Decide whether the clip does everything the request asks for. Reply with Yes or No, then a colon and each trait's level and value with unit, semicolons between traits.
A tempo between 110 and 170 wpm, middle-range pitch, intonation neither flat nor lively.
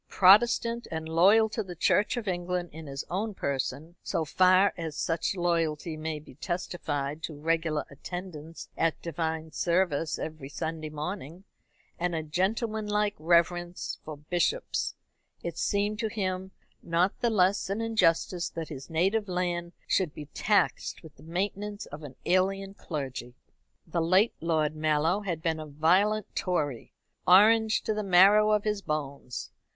Yes: average, 150 wpm; medium, 175 Hz; average, 3.9 semitones